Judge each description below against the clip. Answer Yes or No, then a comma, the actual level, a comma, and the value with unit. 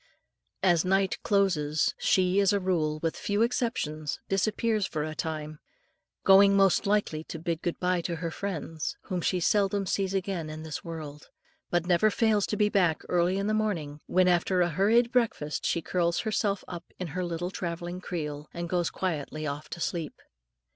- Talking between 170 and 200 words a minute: Yes, average, 180 wpm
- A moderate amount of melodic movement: Yes, average, 3.6 semitones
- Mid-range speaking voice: Yes, medium, 180 Hz